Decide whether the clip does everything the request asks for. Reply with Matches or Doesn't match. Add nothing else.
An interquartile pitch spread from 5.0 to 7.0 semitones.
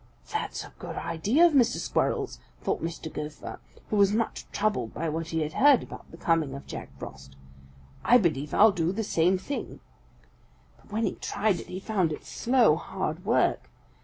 Matches